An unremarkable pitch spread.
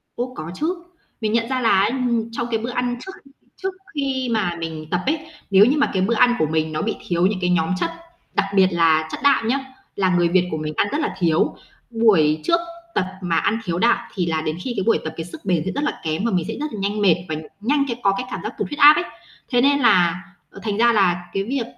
No: wide, 6.1 semitones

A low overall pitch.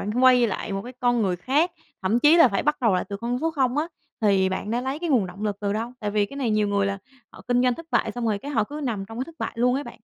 No: high, 235 Hz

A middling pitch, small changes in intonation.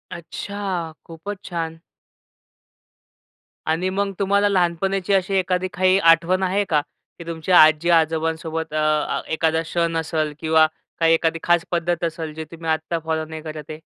Yes: medium, 165 Hz; narrow, 2.3 semitones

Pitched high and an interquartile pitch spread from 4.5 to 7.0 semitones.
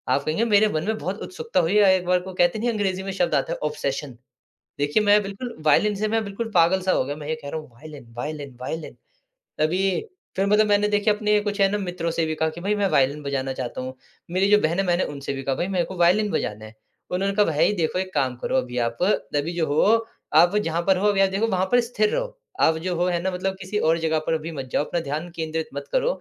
No: medium, 180 Hz; average, 4.8 semitones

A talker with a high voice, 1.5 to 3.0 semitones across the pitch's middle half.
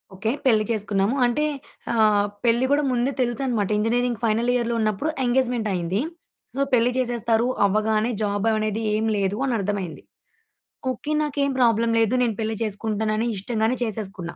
Yes: high, 225 Hz; narrow, 2.4 semitones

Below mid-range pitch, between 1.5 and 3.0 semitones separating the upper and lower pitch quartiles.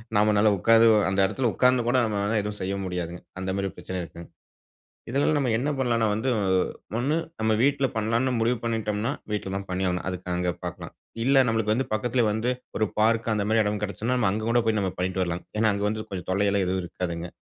No: low, 105 Hz; average, 3.5 semitones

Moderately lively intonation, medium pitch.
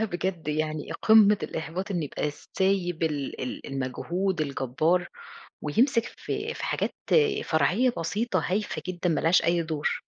Yes: average, 3.9 semitones; medium, 170 Hz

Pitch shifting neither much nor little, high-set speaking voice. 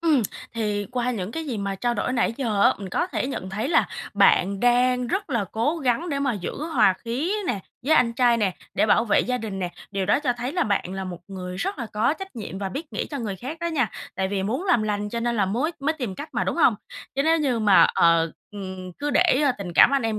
No: wide, 5.9 semitones; high, 235 Hz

